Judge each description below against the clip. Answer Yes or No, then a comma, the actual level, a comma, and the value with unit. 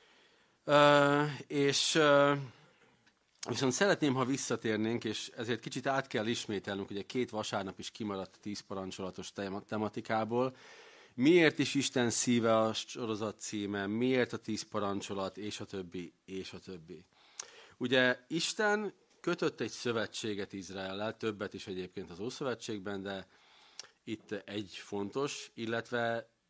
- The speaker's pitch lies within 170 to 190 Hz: No, low, 115 Hz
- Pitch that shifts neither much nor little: Yes, average, 5.0 semitones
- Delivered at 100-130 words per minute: Yes, average, 125 wpm